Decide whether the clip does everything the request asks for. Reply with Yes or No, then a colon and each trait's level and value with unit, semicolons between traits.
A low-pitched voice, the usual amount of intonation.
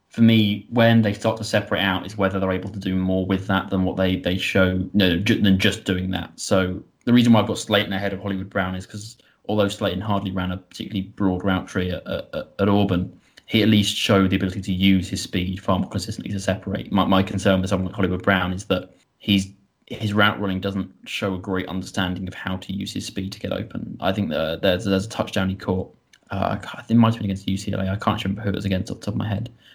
No: very low, 95 Hz; narrow, 1.6 semitones